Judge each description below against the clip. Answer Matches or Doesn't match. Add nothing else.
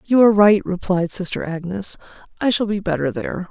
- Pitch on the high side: Matches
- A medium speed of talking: Matches